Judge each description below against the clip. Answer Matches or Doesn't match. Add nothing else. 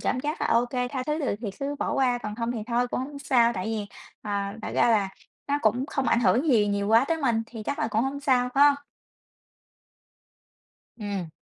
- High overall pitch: Matches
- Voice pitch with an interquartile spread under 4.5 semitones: Matches